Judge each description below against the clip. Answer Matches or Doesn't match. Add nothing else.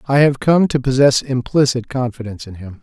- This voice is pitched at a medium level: Doesn't match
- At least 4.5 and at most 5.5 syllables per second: Doesn't match